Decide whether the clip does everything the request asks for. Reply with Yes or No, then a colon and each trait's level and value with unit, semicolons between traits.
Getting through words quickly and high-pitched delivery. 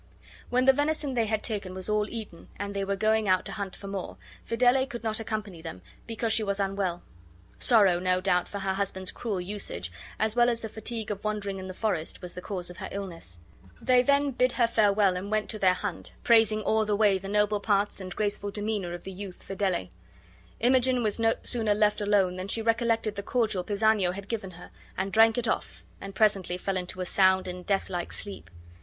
Yes: fast, 215 wpm; high, 205 Hz